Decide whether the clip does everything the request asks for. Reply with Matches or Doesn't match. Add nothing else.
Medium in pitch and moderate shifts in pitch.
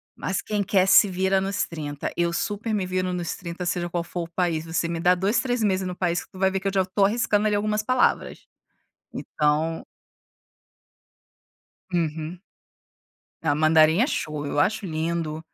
Matches